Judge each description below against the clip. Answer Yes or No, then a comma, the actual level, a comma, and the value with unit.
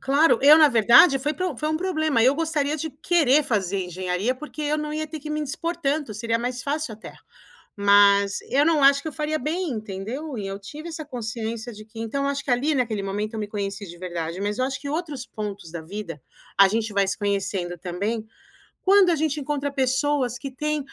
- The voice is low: No, very high, 255 Hz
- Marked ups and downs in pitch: Yes, wide, 6.7 semitones